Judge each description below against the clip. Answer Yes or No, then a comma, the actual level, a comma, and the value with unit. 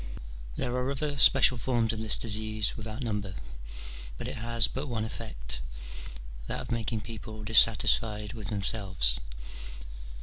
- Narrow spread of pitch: Yes, narrow, 2.0 semitones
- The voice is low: Yes, low, 110 Hz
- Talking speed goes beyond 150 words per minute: No, slow, 135 wpm